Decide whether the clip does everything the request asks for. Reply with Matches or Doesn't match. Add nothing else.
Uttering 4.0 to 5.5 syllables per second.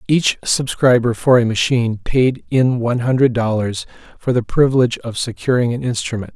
Matches